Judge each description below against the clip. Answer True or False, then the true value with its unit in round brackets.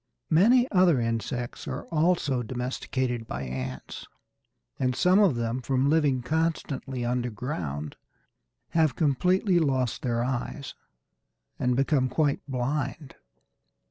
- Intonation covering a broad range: False (4.3 semitones)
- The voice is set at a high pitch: False (130 Hz)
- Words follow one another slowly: True (110 wpm)